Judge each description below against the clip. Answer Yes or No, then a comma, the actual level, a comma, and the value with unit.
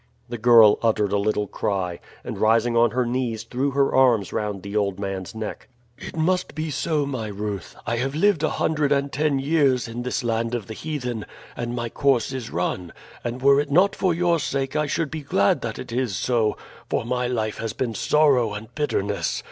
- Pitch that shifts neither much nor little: Yes, average, 4.6 semitones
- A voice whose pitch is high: No, low, 120 Hz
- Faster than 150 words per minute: Yes, fast, 205 wpm